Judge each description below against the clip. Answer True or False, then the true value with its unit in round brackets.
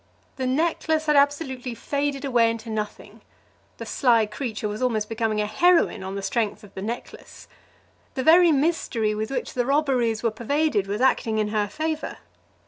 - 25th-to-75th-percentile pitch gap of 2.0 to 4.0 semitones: False (4.9 semitones)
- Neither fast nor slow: True (170 wpm)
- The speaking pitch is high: True (240 Hz)